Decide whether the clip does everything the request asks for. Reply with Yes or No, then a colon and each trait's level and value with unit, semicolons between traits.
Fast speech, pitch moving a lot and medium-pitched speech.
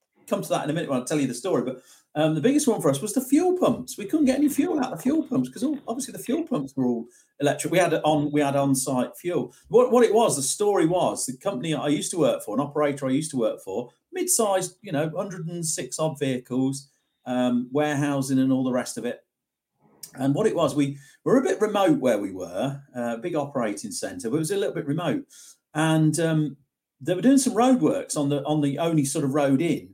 Yes: fast, 250 wpm; wide, 8.2 semitones; medium, 155 Hz